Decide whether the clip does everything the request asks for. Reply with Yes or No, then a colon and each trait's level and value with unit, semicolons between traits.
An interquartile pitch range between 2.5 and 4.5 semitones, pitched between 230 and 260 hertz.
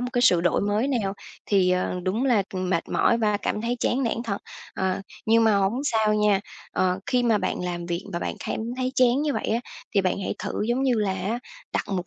No: average, 4.2 semitones; high, 210 Hz